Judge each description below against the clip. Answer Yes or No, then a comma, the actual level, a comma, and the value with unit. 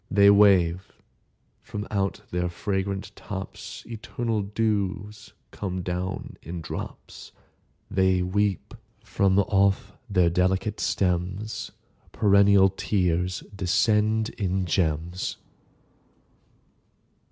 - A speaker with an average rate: No, slow, 80 wpm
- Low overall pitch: Yes, very low, 95 Hz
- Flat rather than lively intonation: Yes, narrow, 2.2 semitones